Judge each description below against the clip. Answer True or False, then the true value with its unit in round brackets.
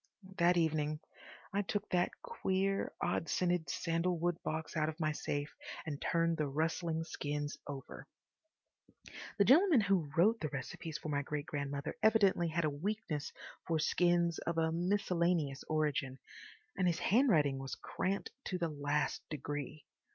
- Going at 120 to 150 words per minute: True (145 wpm)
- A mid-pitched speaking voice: True (165 Hz)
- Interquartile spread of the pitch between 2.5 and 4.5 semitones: True (3.4 semitones)